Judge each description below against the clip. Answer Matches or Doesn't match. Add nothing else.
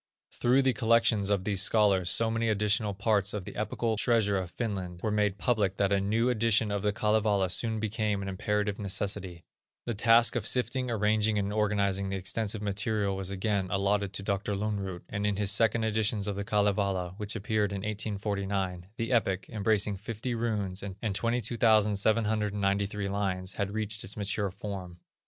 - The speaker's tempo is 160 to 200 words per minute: Matches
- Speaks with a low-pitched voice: Matches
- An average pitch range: Doesn't match